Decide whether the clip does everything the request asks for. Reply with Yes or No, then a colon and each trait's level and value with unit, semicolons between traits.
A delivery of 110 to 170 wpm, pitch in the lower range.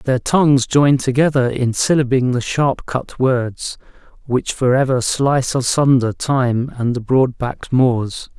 Yes: average, 150 wpm; low, 130 Hz